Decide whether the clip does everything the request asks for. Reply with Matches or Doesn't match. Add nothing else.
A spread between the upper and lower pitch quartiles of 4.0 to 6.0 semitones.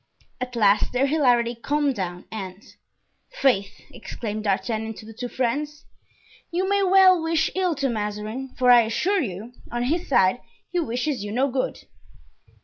Matches